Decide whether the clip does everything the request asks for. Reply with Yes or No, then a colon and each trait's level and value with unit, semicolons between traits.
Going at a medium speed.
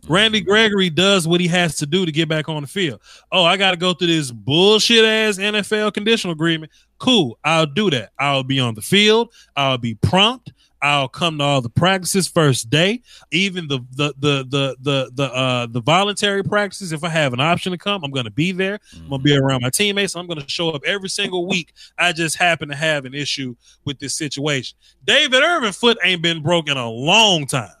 No: fast, 220 wpm